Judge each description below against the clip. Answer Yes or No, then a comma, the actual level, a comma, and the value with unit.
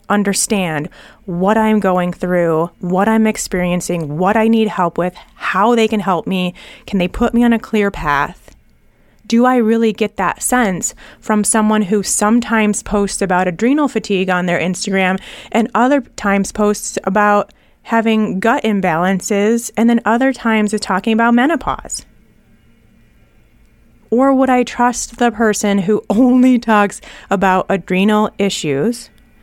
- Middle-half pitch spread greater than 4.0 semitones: No, average, 3.4 semitones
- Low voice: No, high, 210 Hz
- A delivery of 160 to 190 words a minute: No, average, 145 wpm